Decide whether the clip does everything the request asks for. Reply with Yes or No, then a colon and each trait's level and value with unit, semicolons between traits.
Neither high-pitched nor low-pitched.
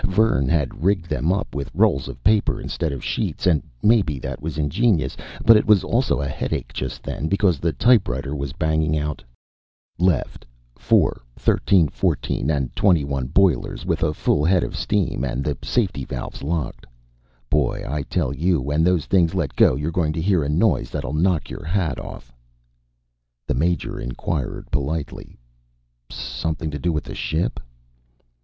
No: very low, 80 Hz